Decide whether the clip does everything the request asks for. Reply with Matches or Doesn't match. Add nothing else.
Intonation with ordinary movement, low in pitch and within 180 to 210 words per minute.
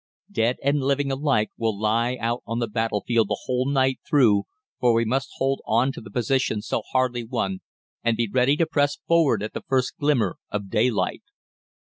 Matches